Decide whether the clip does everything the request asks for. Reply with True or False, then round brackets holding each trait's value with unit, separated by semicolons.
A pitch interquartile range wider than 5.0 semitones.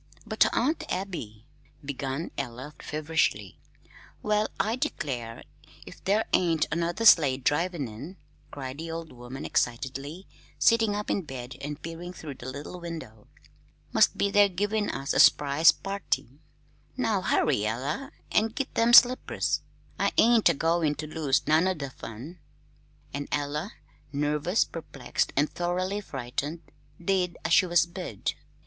True (5.5 semitones)